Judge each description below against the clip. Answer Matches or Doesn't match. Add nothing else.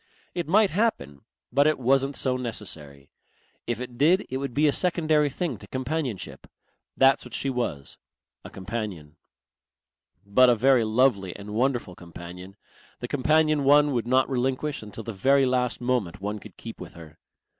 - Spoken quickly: Doesn't match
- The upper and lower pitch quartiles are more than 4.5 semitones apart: Matches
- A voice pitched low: Matches